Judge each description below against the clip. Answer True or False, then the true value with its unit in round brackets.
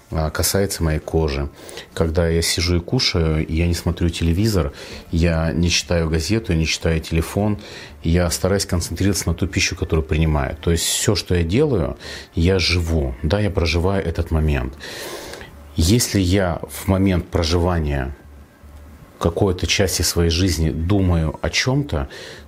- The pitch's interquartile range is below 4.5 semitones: True (3.1 semitones)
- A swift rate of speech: False (140 wpm)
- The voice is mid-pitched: False (85 Hz)